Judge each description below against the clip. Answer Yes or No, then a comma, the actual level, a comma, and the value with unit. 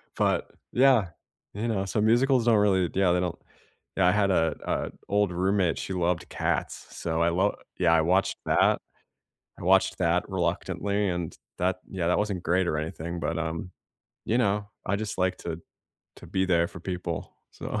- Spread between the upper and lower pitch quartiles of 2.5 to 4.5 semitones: Yes, average, 3.1 semitones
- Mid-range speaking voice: No, very low, 95 Hz